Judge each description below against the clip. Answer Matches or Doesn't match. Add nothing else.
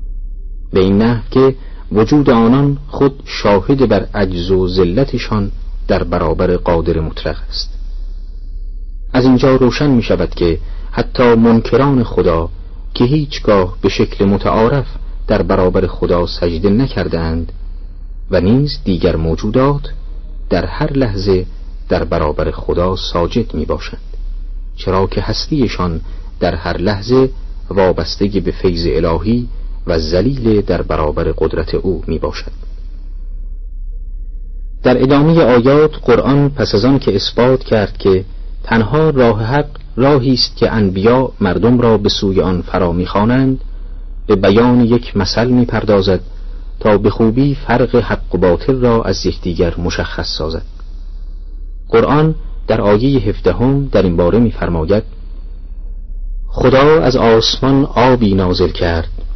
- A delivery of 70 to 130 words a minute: Matches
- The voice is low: Matches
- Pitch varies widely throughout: Matches